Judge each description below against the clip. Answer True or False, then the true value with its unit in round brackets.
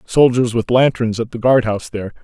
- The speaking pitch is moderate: False (115 Hz)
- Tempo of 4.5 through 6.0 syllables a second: True (5.9 syllables/s)